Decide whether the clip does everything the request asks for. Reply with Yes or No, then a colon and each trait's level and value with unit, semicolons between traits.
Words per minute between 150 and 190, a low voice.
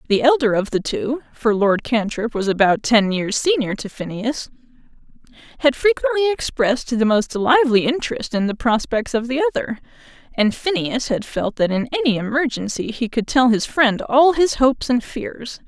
No: average, 170 wpm; high, 245 Hz